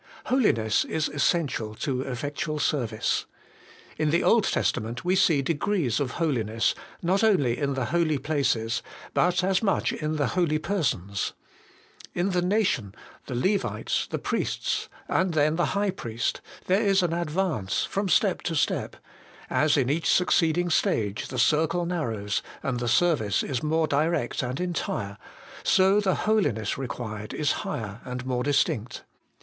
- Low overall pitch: No, medium, 150 Hz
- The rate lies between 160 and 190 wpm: No, average, 150 wpm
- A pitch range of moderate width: No, wide, 6.4 semitones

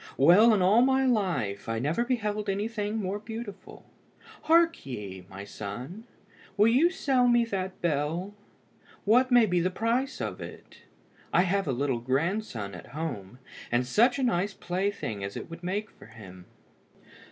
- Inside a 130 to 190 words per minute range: Yes, average, 160 wpm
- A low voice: No, high, 190 Hz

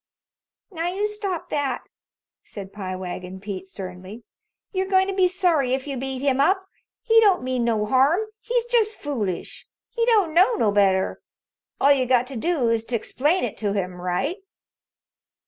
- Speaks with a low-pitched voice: No, very high, 270 Hz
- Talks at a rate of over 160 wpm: Yes, average, 170 wpm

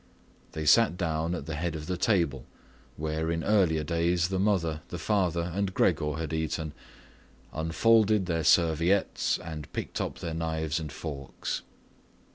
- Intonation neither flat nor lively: No, narrow, 2.2 semitones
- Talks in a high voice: No, very low, 80 Hz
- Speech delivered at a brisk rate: No, average, 150 wpm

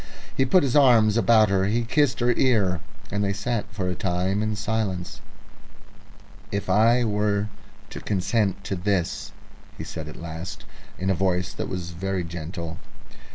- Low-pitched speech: Yes, low, 100 Hz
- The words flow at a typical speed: Yes, average, 160 wpm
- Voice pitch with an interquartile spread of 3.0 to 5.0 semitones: Yes, average, 3.3 semitones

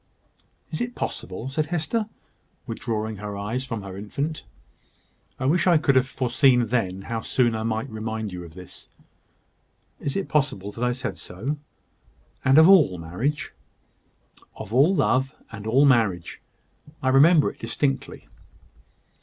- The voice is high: No, low, 125 Hz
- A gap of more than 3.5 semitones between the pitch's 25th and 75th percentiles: Yes, average, 5.2 semitones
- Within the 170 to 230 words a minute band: No, average, 145 wpm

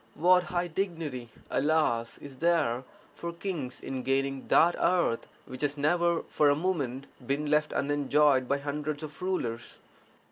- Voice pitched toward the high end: No, medium, 150 Hz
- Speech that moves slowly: No, average, 145 wpm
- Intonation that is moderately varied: Yes, average, 4.0 semitones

